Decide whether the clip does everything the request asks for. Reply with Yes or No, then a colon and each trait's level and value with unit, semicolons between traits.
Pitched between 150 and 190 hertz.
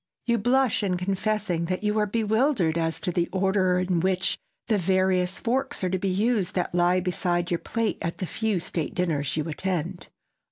Yes: medium, 185 Hz